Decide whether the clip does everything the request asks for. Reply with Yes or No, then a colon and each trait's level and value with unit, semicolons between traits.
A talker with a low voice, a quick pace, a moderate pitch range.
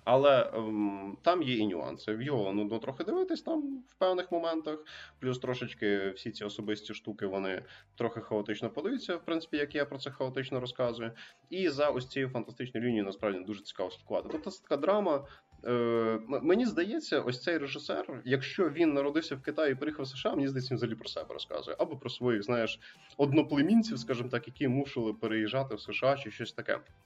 Yes: low, 125 Hz; fast, 180 wpm; average, 4.7 semitones